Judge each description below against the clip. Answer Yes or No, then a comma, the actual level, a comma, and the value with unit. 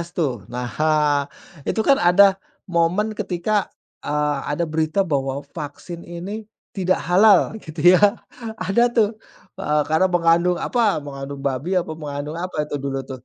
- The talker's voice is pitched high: No, medium, 170 Hz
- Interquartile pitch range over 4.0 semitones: Yes, average, 4.7 semitones